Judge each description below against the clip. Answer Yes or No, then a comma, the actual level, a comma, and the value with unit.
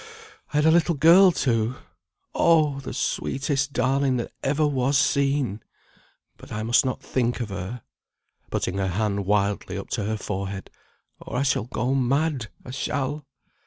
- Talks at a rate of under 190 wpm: Yes, average, 160 wpm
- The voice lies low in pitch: Yes, low, 130 Hz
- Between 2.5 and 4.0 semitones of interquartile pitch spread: No, average, 4.6 semitones